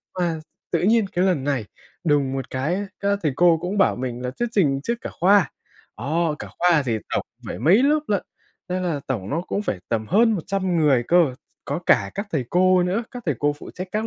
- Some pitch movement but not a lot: No, wide, 5.8 semitones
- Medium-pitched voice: Yes, medium, 175 Hz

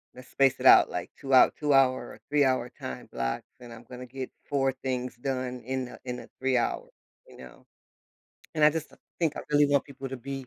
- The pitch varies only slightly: Yes, narrow, 1.7 semitones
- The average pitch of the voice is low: Yes, low, 130 Hz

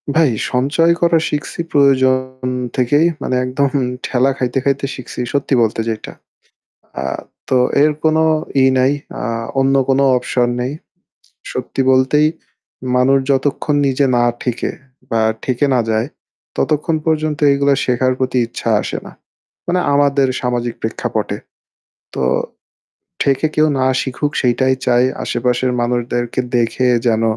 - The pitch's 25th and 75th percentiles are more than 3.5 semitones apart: No, narrow, 2.4 semitones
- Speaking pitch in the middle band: No, low, 130 Hz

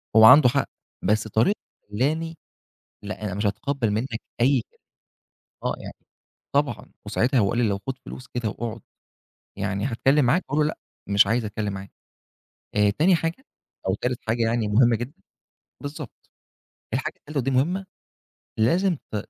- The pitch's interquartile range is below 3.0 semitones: No, average, 4.9 semitones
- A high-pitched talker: No, low, 120 Hz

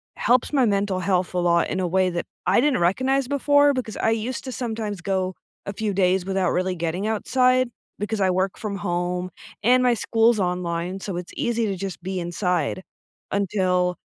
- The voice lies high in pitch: Yes, high, 195 Hz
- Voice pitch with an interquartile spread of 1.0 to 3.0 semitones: No, average, 4.0 semitones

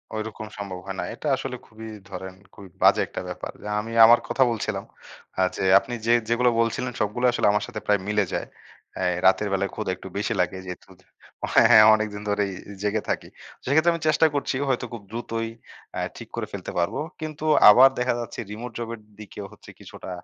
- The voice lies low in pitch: Yes, low, 110 Hz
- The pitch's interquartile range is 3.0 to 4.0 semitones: Yes, average, 3.3 semitones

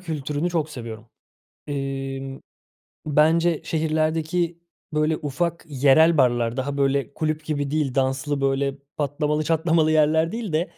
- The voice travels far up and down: No, narrow, 2.6 semitones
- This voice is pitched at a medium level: Yes, medium, 150 Hz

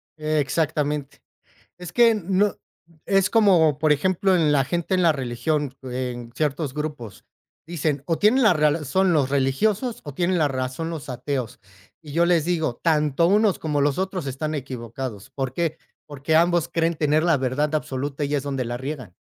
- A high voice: No, medium, 150 Hz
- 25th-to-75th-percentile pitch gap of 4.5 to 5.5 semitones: No, average, 4.1 semitones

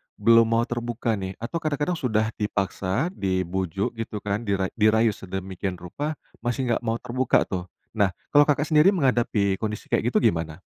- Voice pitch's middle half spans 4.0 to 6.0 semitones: Yes, average, 4.4 semitones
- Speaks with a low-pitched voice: Yes, low, 110 Hz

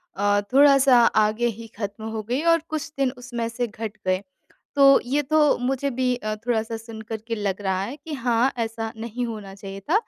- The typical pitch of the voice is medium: No, high, 230 Hz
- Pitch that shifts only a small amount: No, average, 3.8 semitones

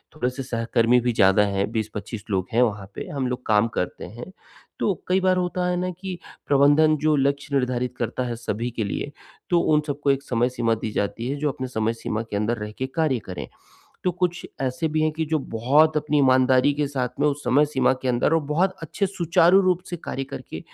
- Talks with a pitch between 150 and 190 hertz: No, low, 135 Hz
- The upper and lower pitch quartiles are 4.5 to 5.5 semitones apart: Yes, average, 4.9 semitones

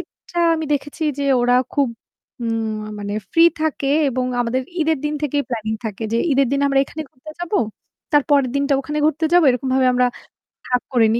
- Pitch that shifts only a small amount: No, average, 3.5 semitones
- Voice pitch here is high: Yes, very high, 270 Hz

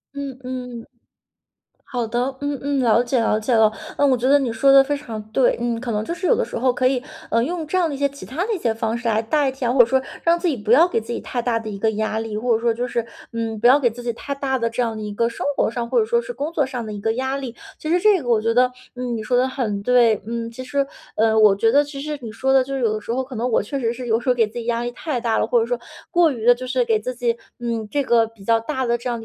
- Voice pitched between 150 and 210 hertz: No, high, 245 Hz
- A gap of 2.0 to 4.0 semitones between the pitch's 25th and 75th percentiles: Yes, average, 3.2 semitones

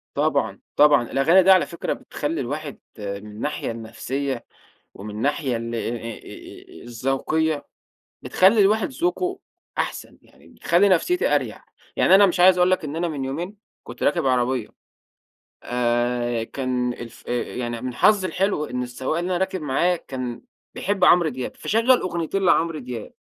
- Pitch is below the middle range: No, medium, 145 Hz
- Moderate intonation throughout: No, wide, 6.8 semitones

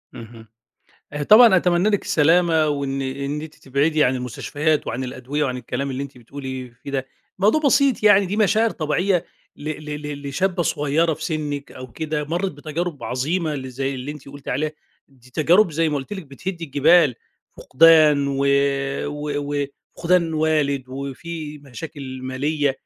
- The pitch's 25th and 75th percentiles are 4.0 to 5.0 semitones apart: No, average, 3.3 semitones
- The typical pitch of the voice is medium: Yes, medium, 150 Hz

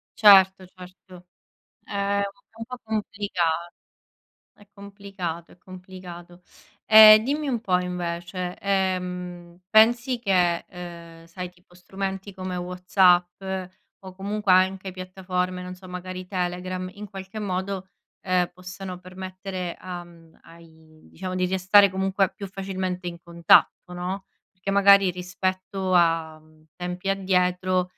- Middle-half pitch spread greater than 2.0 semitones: No, narrow, 1.4 semitones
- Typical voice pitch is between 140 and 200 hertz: Yes, medium, 185 Hz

